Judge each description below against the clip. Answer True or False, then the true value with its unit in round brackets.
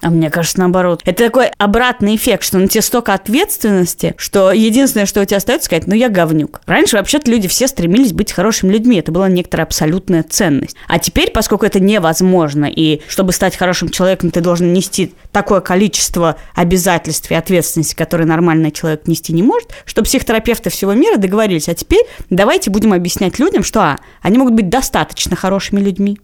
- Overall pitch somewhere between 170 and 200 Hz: True (190 Hz)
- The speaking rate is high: True (180 wpm)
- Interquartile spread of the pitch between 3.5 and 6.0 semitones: True (4.3 semitones)